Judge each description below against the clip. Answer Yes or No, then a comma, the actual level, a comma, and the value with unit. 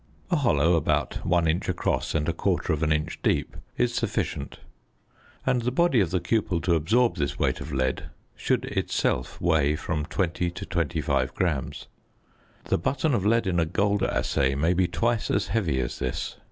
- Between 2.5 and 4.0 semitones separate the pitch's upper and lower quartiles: No, average, 4.9 semitones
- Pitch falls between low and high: No, very low, 85 Hz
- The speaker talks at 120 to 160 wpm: No, average, 170 wpm